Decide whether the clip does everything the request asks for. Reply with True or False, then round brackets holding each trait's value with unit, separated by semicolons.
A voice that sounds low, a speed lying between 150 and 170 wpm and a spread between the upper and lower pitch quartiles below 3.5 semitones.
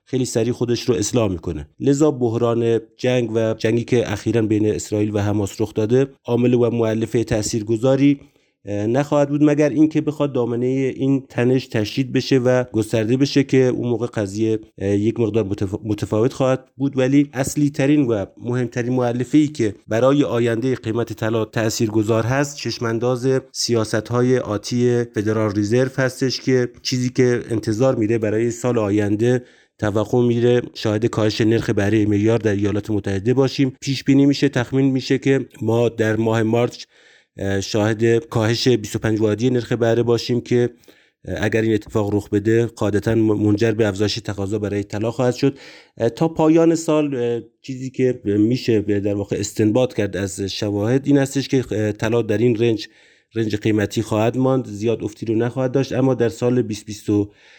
True (115 Hz; 155 wpm; 3.0 semitones)